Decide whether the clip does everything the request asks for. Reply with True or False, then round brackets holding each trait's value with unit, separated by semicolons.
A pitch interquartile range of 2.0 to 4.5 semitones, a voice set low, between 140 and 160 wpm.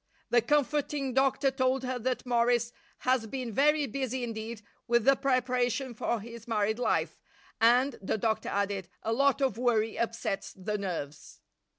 False (3.0 semitones; 240 Hz; 155 wpm)